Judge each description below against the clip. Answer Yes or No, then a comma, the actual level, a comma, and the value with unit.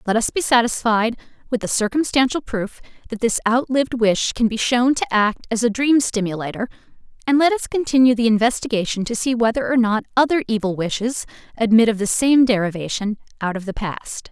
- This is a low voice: No, high, 230 Hz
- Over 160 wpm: Yes, average, 185 wpm